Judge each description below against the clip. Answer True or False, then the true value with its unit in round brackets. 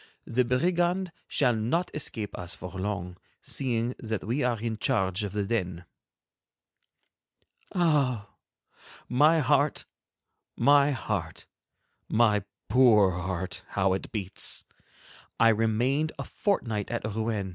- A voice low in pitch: True (115 Hz)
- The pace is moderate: False (115 wpm)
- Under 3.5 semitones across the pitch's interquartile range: False (5.1 semitones)